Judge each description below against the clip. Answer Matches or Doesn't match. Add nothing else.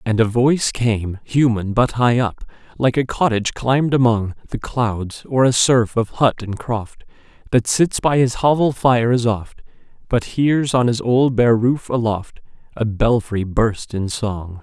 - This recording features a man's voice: Matches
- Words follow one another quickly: Doesn't match